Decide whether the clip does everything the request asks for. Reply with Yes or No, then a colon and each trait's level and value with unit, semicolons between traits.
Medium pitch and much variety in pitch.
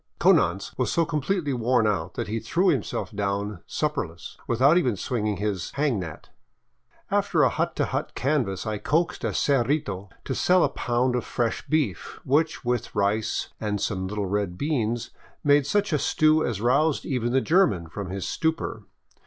No: low, 120 Hz; wide, 6.4 semitones